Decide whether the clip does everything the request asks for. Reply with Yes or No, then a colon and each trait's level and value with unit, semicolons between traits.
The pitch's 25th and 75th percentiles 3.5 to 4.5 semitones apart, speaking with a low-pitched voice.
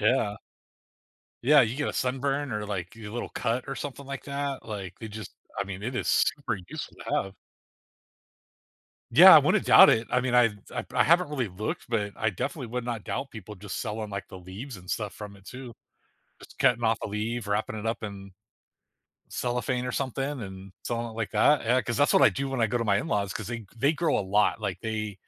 Yes: average, 3.8 semitones; low, 115 Hz